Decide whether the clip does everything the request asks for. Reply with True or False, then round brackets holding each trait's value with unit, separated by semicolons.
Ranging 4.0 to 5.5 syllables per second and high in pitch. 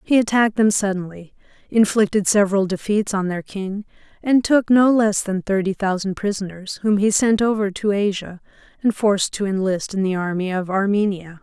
True (5.2 syllables/s; 200 Hz)